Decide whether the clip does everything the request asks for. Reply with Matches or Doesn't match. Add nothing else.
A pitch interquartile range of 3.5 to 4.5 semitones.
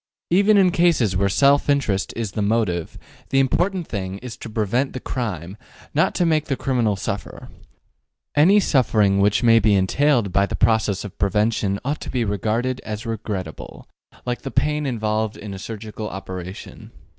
Doesn't match